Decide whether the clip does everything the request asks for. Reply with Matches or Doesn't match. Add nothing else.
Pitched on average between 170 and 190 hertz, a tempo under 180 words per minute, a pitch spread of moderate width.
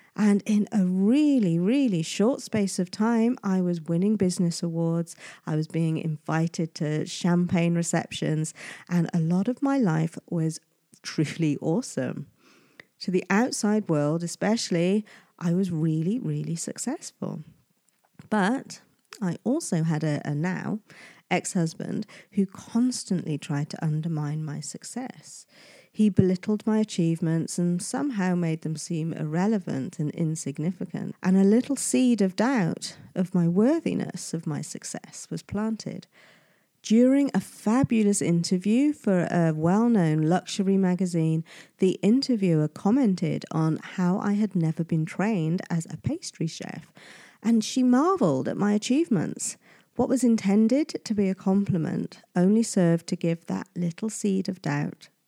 Matches